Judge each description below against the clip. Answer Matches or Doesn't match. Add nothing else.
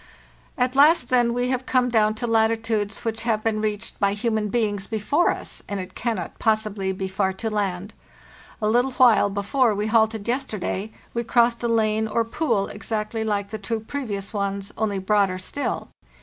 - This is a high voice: Matches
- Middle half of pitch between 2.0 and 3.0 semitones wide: Matches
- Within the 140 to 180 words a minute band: Matches